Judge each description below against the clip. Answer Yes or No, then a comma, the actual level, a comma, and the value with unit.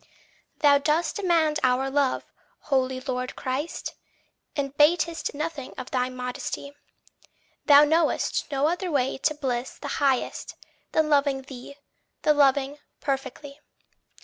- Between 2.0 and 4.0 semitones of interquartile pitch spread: Yes, narrow, 2.4 semitones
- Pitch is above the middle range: Yes, very high, 280 Hz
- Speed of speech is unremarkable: No, slow, 125 wpm